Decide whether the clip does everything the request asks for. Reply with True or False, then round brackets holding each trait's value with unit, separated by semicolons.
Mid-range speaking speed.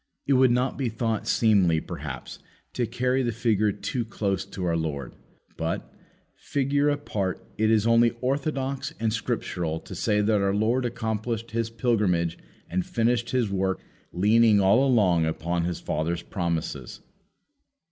True (145 wpm)